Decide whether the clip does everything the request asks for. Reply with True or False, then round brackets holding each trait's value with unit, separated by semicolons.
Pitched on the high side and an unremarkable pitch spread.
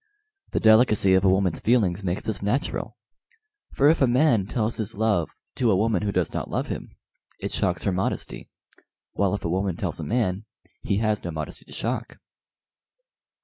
False (105 Hz; 3.4 semitones)